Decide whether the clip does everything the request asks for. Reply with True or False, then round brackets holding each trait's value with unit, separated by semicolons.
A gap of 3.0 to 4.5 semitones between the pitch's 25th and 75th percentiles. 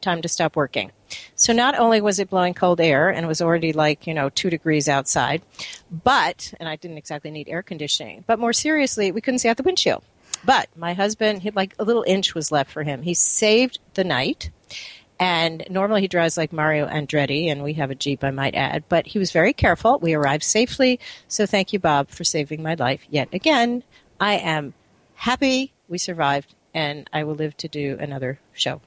False (5.3 semitones)